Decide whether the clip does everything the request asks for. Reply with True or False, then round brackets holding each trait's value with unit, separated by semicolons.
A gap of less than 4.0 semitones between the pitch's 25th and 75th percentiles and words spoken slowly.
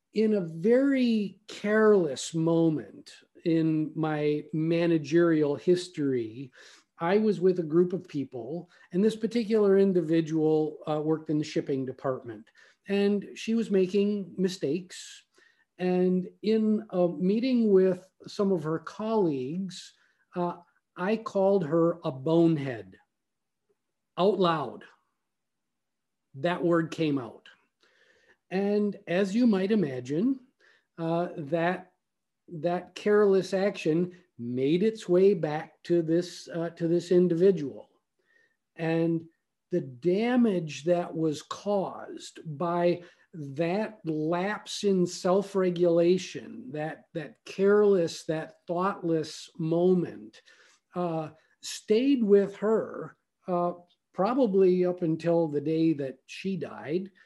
True (3.6 semitones; 105 wpm)